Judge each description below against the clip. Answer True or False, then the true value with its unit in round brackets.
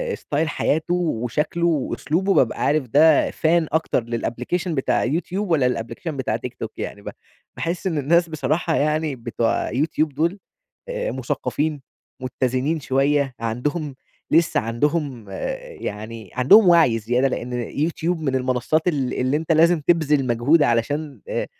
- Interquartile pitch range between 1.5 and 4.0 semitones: False (4.5 semitones)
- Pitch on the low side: False (145 Hz)